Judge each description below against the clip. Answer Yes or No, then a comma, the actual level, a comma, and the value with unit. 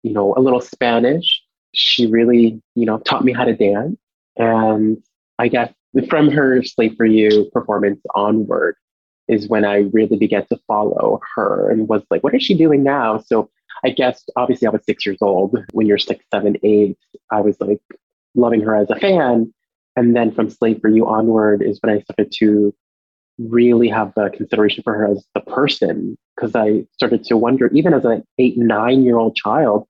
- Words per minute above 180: Yes, average, 195 wpm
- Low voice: Yes, low, 110 Hz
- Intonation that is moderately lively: No, narrow, 2.3 semitones